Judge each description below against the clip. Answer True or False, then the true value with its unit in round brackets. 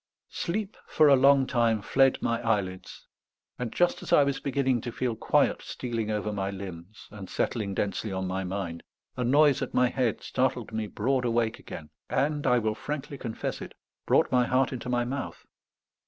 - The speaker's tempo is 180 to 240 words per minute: True (185 wpm)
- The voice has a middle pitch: False (120 Hz)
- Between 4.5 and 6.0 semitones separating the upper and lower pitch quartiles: False (4.1 semitones)